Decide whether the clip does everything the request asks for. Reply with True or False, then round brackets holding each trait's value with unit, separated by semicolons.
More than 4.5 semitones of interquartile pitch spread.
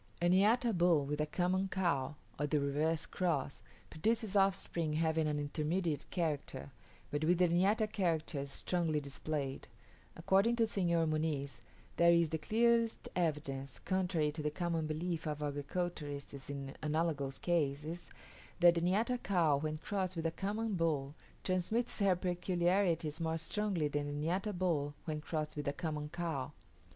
False (3.6 semitones)